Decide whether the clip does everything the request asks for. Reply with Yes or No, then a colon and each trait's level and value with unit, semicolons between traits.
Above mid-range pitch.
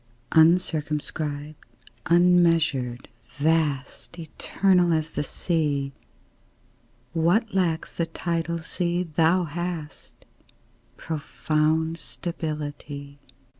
No: medium, 160 Hz